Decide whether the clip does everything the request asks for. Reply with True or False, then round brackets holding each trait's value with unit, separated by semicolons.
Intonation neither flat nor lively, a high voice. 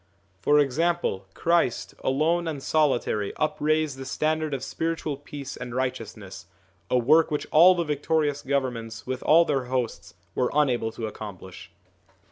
False (4.3 semitones; 140 Hz)